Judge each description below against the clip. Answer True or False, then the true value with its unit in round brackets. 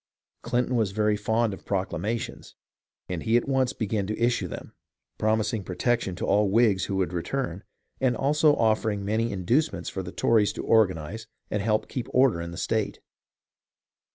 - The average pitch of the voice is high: False (110 Hz)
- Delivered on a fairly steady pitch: False (3.4 semitones)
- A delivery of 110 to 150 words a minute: False (165 wpm)